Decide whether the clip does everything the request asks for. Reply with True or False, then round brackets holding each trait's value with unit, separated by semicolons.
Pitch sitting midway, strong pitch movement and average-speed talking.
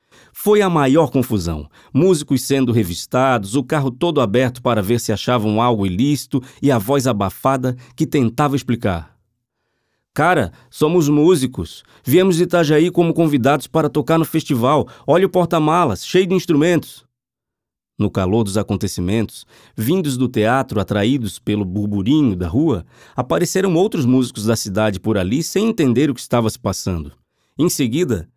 False (130 Hz; 5.9 semitones; 150 wpm)